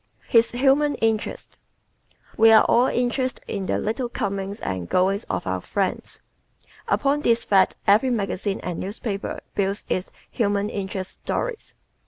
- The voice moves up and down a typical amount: Yes, average, 3.7 semitones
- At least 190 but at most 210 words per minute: No, average, 145 wpm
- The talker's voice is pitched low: No, high, 210 Hz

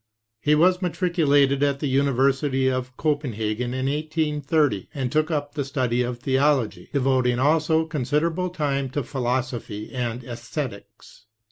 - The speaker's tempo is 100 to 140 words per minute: Yes, slow, 135 wpm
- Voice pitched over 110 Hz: Yes, low, 135 Hz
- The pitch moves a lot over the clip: No, average, 3.3 semitones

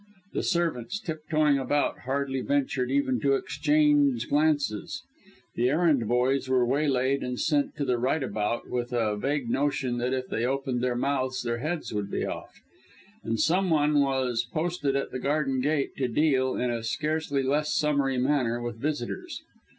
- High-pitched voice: No, low, 135 Hz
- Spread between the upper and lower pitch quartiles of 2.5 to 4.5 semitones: Yes, average, 3.0 semitones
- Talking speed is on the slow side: No, average, 165 wpm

